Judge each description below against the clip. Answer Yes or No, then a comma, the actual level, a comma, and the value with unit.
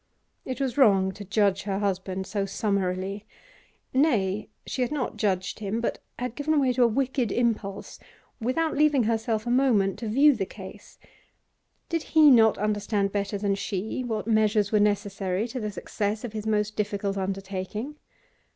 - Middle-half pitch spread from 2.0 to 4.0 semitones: Yes, average, 3.6 semitones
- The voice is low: No, high, 210 Hz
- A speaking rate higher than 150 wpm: Yes, average, 165 wpm